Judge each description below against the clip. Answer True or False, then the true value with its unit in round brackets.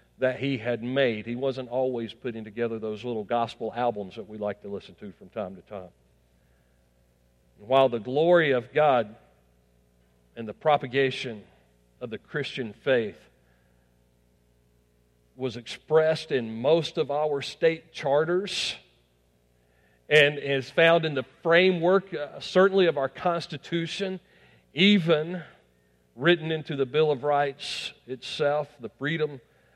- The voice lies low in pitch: True (125 Hz)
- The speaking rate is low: True (130 wpm)